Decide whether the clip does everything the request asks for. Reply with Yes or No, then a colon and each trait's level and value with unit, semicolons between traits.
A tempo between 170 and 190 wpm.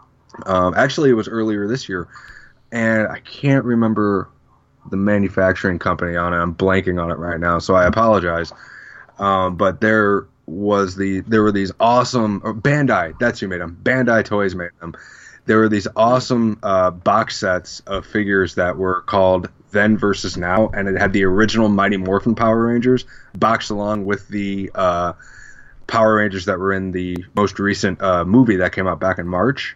Yes: average, 180 wpm